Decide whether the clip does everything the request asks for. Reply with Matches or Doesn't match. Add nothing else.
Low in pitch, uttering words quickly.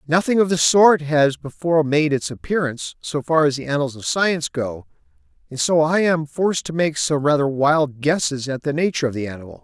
Doesn't match